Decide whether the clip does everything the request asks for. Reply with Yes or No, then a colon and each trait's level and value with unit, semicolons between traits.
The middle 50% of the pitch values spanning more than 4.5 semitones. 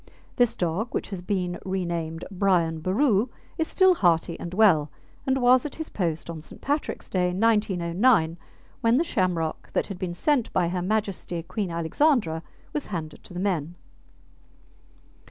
Yes: average, 5.2 semitones